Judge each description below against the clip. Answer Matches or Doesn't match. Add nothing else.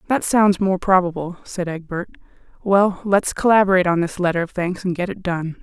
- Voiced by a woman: Matches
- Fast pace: Doesn't match